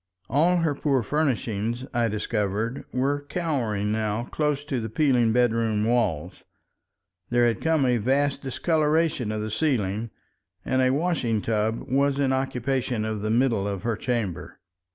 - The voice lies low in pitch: Yes, low, 120 Hz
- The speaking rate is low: No, average, 150 wpm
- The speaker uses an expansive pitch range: No, average, 4.3 semitones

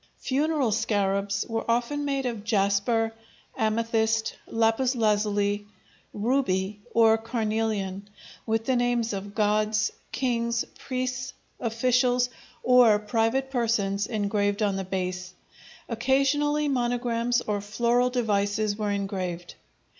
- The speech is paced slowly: Yes, slow, 105 wpm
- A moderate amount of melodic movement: Yes, average, 3.1 semitones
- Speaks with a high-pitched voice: Yes, high, 225 Hz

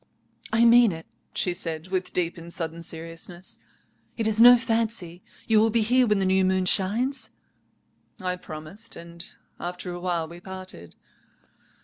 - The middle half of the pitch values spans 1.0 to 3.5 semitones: No, average, 4.6 semitones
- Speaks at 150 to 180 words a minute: Yes, average, 155 wpm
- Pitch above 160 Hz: Yes, medium, 185 Hz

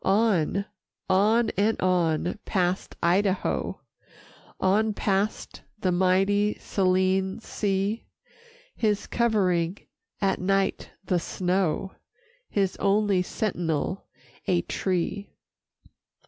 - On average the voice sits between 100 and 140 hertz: No, high, 190 Hz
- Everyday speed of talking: No, slow, 85 wpm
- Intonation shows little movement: Yes, narrow, 2.0 semitones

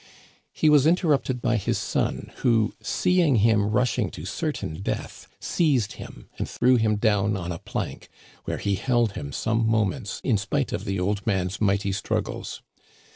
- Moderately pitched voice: No, low, 110 Hz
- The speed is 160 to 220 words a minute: Yes, average, 170 wpm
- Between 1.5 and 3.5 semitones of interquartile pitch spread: No, average, 4.3 semitones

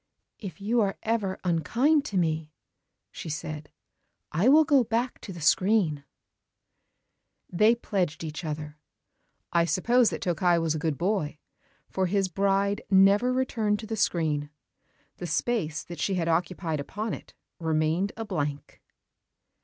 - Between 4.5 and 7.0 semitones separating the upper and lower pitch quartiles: Yes, average, 5.1 semitones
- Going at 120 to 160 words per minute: Yes, average, 145 wpm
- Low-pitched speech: No, medium, 185 Hz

